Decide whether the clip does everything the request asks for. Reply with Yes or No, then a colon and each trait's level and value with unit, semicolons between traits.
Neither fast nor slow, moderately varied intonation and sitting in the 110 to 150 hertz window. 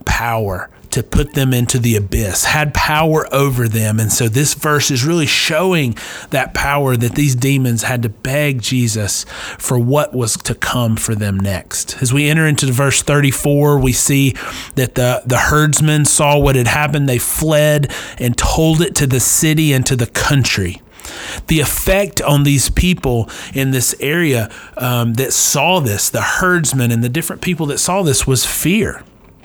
Yes: average, 175 wpm; average, 3.9 semitones; low, 135 Hz